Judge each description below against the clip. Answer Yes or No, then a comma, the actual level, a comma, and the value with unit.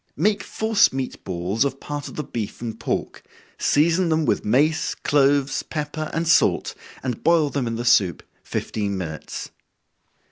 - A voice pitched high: No, medium, 140 Hz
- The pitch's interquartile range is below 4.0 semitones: No, wide, 5.5 semitones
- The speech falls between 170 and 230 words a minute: No, average, 155 wpm